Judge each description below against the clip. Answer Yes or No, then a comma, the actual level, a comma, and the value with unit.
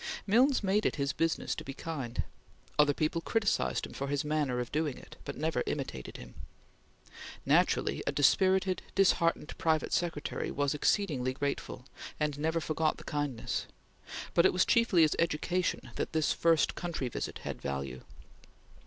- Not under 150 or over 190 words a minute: Yes, average, 155 wpm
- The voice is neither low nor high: Yes, medium, 155 Hz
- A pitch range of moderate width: Yes, average, 3.6 semitones